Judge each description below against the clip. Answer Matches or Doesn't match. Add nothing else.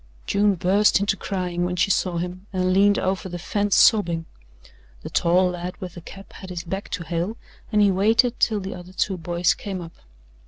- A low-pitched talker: Doesn't match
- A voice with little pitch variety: Matches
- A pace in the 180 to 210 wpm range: Matches